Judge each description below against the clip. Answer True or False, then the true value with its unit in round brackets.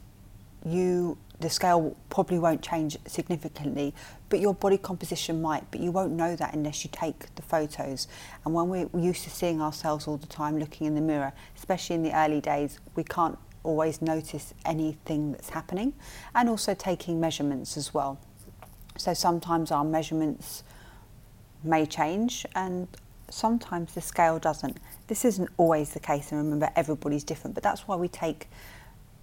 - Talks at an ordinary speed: True (160 wpm)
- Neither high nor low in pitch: True (155 Hz)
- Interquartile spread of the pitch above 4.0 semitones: False (3.1 semitones)